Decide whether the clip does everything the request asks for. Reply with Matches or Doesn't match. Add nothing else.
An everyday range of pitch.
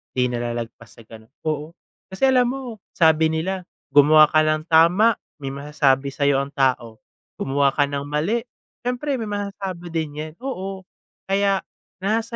Doesn't match